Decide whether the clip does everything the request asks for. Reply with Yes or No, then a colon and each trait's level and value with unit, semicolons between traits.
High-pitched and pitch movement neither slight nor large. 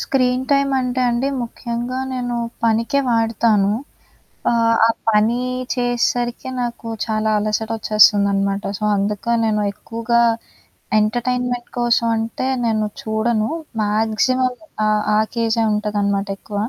No: high, 230 Hz; narrow, 2.3 semitones